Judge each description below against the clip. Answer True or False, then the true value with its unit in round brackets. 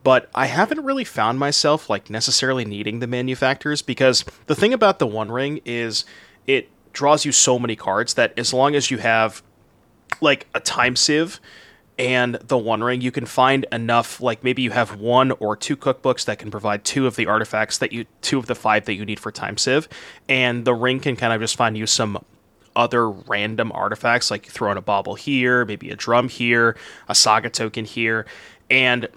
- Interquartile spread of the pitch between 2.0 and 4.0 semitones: True (3.0 semitones)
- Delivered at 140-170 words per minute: False (200 wpm)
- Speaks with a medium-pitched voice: False (125 Hz)